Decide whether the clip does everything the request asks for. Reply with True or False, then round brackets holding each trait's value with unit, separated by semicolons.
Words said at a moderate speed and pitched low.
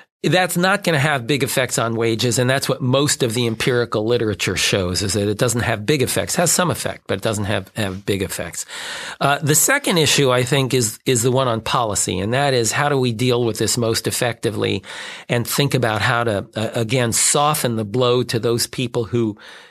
False (220 wpm; 120 Hz)